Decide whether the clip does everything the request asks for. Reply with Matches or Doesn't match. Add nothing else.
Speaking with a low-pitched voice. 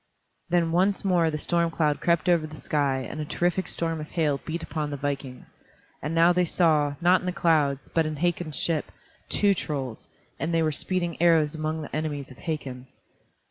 Doesn't match